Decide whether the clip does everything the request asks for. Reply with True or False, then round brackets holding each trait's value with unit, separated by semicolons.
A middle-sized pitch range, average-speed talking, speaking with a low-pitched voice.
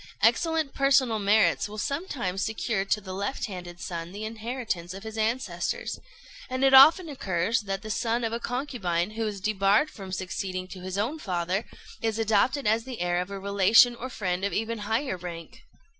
False (4.3 semitones; 185 wpm; 215 Hz)